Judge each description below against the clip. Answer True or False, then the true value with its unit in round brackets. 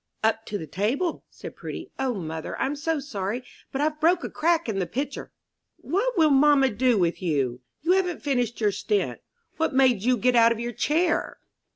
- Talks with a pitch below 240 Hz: False (255 Hz)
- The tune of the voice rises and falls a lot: True (6.6 semitones)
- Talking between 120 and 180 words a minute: False (195 wpm)